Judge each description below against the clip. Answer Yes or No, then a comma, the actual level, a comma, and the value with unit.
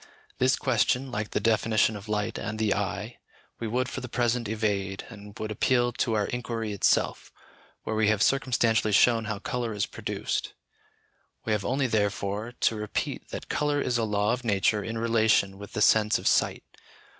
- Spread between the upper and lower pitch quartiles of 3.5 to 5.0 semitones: No, narrow, 2.5 semitones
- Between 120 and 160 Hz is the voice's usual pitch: No, low, 110 Hz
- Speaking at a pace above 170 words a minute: Yes, average, 180 wpm